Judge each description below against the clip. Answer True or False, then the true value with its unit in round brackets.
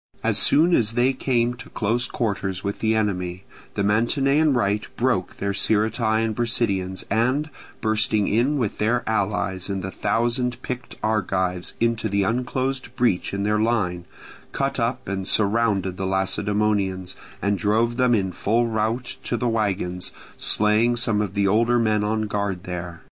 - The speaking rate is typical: True (160 wpm)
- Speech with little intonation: False (3.2 semitones)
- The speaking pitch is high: False (110 Hz)